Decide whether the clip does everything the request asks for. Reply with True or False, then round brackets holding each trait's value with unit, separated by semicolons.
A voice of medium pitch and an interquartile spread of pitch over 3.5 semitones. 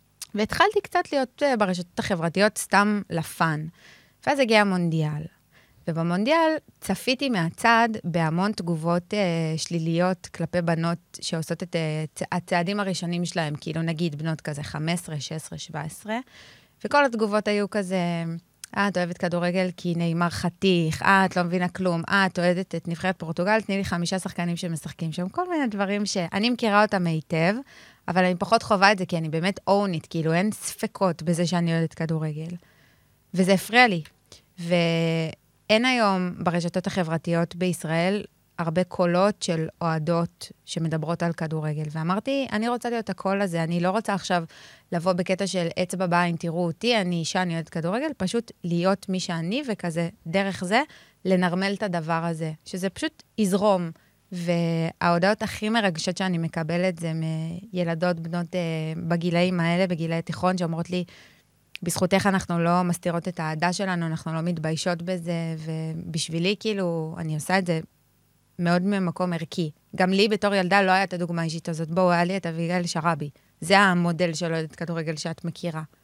False (175 Hz; 2.8 semitones)